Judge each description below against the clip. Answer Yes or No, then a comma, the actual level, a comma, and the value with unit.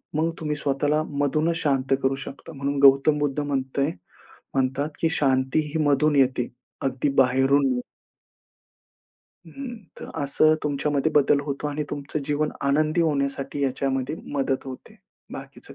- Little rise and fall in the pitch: Yes, narrow, 1.9 semitones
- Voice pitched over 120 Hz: Yes, medium, 140 Hz